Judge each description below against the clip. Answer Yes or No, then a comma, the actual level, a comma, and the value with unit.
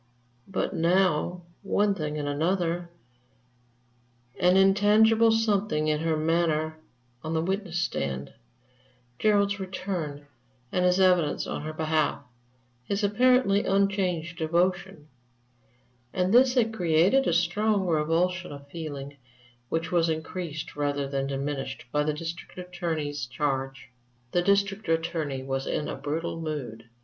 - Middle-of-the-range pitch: Yes, medium, 170 Hz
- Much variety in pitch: No, average, 4.2 semitones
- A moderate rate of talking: No, slow, 125 wpm